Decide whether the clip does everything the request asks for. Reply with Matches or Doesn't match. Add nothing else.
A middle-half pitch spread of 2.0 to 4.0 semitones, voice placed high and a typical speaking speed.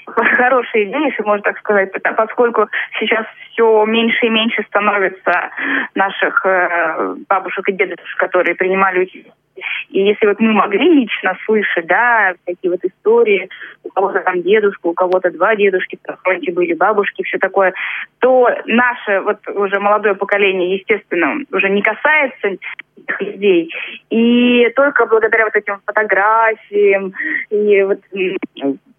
Matches